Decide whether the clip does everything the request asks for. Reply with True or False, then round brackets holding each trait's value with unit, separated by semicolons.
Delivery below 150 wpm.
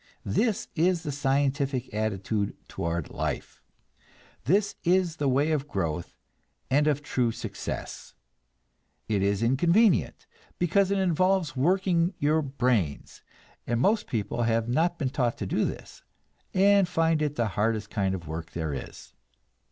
True (140 wpm)